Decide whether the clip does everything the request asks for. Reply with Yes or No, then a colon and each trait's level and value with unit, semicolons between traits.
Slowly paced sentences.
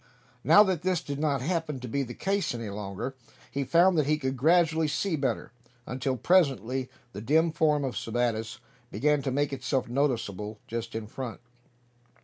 No: average, 170 wpm